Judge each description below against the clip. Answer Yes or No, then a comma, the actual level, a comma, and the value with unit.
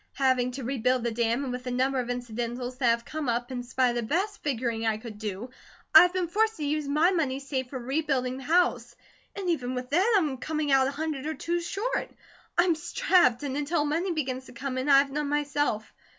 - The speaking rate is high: Yes, fast, 235 wpm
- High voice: Yes, very high, 270 Hz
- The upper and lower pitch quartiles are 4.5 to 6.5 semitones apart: No, average, 3.9 semitones